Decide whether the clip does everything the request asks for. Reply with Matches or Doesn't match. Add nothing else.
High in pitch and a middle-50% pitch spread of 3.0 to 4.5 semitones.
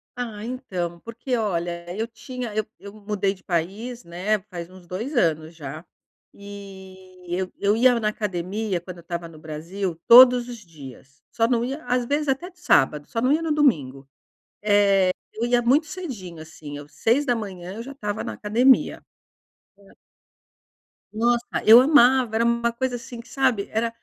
Doesn't match